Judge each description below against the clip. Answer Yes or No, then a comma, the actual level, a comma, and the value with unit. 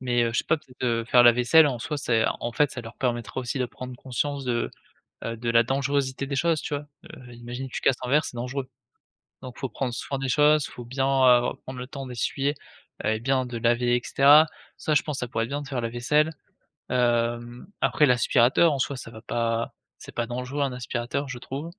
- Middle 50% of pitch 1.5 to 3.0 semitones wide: Yes, narrow, 2.6 semitones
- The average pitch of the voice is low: Yes, low, 125 Hz